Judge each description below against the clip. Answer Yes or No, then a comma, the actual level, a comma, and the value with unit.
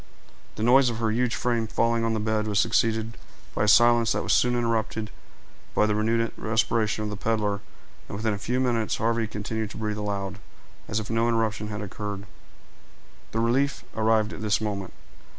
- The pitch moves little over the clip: Yes, narrow, 1.6 semitones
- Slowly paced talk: No, average, 185 wpm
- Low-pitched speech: Yes, low, 110 Hz